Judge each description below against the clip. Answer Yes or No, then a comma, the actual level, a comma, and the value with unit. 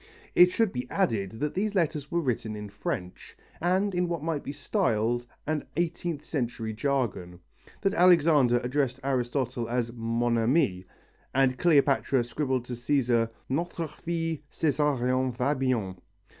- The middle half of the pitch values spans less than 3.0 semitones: No, average, 5.2 semitones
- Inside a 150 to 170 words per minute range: No, average, 140 wpm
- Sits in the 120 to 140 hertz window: Yes, low, 135 Hz